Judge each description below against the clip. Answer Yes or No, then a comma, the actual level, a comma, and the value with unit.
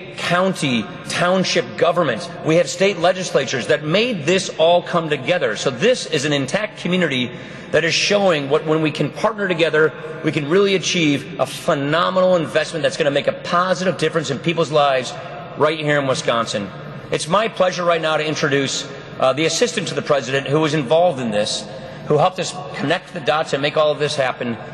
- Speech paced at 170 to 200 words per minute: Yes, average, 190 wpm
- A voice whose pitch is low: No, medium, 165 Hz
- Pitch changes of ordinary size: Yes, average, 3.1 semitones